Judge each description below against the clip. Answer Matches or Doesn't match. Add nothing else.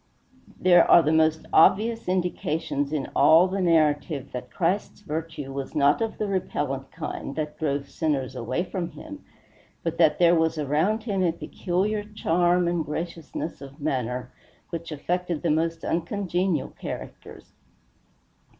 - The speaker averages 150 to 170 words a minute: Doesn't match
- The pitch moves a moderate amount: Matches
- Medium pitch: Matches